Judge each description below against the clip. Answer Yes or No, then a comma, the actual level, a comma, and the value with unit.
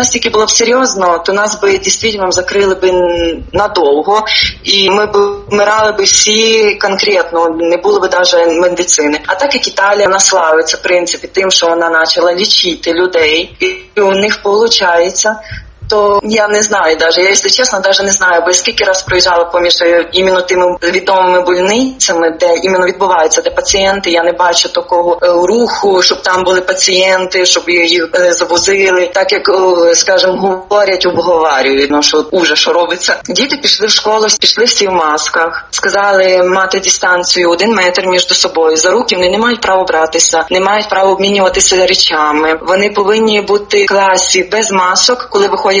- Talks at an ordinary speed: No, fast, 165 wpm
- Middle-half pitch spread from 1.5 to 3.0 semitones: Yes, average, 2.7 semitones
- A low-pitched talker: No, medium, 185 Hz